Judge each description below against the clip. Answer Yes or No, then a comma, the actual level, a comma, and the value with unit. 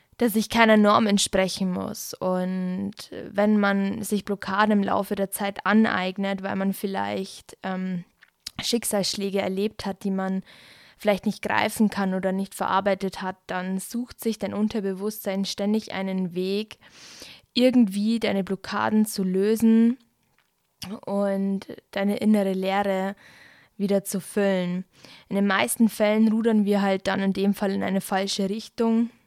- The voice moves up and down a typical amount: No, narrow, 1.8 semitones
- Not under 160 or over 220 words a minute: No, average, 140 wpm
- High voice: Yes, high, 200 Hz